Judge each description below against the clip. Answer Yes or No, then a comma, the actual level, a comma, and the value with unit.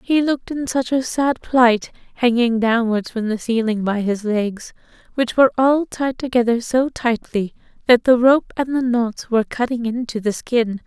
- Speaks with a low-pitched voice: No, high, 240 Hz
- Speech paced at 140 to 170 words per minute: No, average, 180 wpm